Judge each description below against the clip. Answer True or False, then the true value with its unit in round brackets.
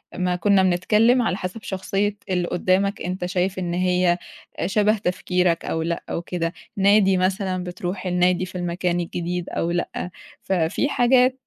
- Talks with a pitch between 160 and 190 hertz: True (185 Hz)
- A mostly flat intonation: True (1.8 semitones)